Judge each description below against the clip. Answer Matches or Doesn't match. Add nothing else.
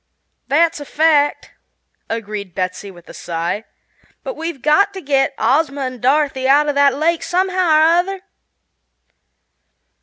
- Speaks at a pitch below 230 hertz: Doesn't match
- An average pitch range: Matches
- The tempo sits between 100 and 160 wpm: Matches